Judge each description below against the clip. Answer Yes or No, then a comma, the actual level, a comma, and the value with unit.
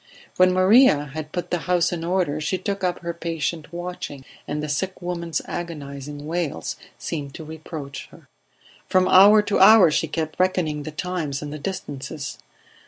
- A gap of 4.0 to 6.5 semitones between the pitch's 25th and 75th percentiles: No, average, 3.4 semitones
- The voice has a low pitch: No, medium, 165 Hz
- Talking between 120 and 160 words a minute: No, average, 170 wpm